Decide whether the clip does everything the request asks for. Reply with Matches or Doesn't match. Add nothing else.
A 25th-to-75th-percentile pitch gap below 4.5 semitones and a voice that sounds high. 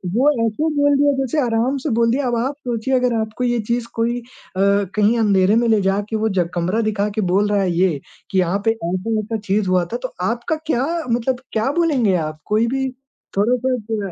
Matches